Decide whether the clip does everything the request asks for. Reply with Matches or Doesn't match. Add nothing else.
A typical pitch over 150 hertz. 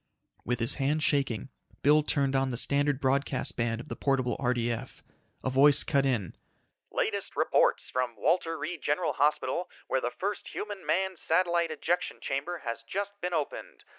Doesn't match